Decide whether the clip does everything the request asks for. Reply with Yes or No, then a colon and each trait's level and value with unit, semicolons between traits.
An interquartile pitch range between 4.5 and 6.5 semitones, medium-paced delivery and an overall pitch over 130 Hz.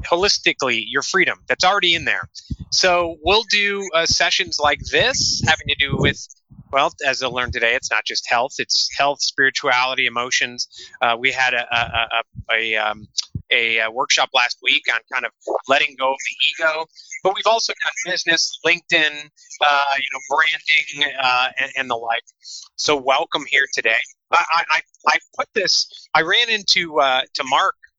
Yes: average, 5.1 semitones; average, 170 wpm; medium, 140 Hz